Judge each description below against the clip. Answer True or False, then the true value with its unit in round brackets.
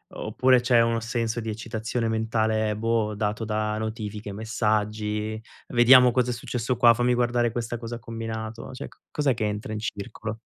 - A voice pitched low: True (115 Hz)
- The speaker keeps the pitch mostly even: True (1.7 semitones)